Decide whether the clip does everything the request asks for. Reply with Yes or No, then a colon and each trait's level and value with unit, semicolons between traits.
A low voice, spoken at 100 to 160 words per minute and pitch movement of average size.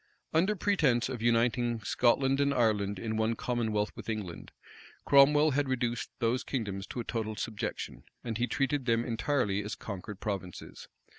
Yes: low, 120 Hz; average, 155 wpm; average, 3.6 semitones